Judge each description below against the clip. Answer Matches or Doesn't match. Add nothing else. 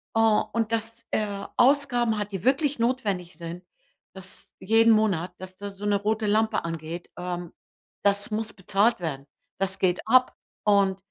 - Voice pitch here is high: Matches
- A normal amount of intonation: Matches